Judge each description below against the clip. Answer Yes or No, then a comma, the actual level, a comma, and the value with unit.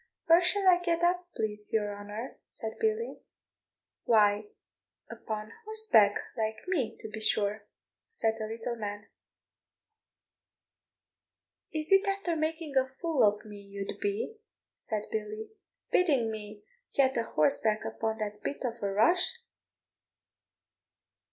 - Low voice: No, high, 225 Hz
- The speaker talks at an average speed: No, slow, 125 wpm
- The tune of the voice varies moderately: No, wide, 8.4 semitones